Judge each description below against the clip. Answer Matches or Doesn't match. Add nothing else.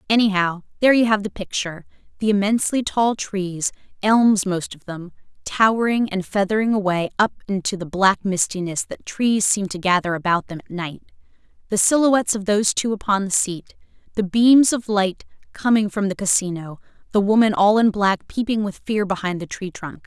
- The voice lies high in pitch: Matches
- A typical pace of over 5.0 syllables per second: Matches